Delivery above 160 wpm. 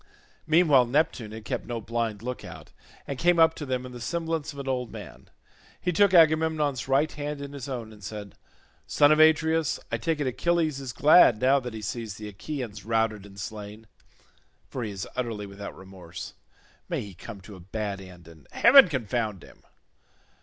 Yes: average, 190 wpm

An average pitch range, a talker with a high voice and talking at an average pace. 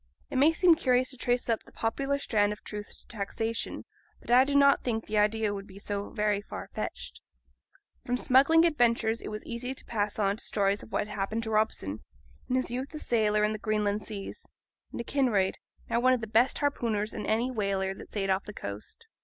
No: average, 3.4 semitones; high, 220 Hz; fast, 220 wpm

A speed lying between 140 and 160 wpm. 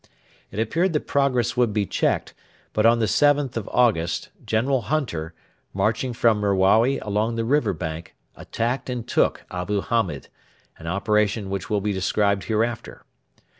Yes: average, 150 wpm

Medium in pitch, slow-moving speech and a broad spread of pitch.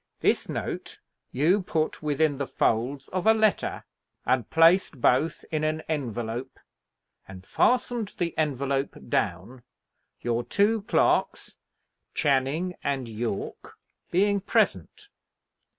Yes: medium, 145 Hz; slow, 110 wpm; wide, 6.3 semitones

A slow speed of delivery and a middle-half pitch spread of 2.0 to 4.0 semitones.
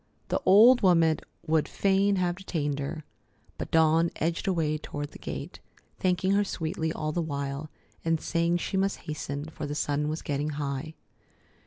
No: average, 165 wpm; average, 3.2 semitones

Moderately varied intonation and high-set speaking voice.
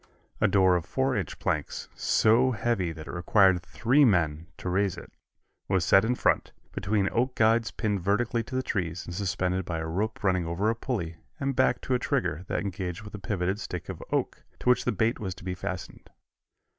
No: average, 4.2 semitones; low, 100 Hz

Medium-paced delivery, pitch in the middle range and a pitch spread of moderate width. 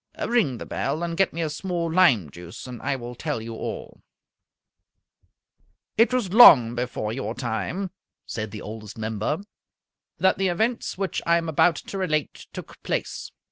No: average, 165 wpm; medium, 150 Hz; wide, 8.3 semitones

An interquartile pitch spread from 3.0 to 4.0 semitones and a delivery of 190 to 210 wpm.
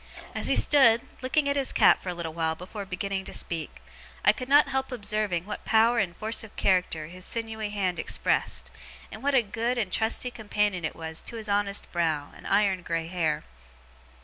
No: average, 4.8 semitones; average, 200 wpm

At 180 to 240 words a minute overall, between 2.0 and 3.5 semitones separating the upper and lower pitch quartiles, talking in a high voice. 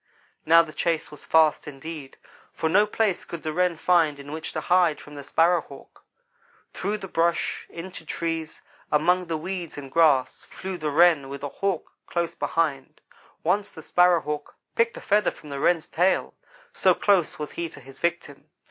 No: average, 185 wpm; average, 3.0 semitones; medium, 165 Hz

